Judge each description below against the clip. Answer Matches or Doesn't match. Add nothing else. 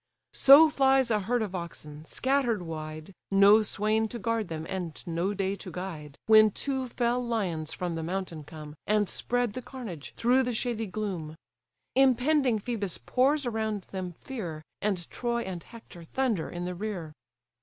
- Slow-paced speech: Doesn't match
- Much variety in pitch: Matches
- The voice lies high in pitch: Matches